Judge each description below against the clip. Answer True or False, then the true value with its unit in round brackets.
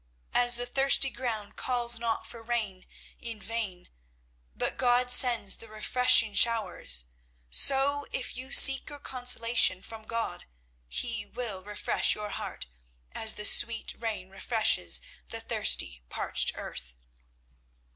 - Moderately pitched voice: False (230 Hz)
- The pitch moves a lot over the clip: False (2.9 semitones)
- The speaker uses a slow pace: True (125 wpm)